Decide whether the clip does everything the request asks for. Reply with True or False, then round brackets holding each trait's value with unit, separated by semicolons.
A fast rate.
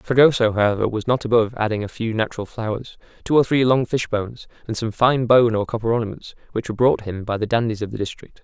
True (235 wpm)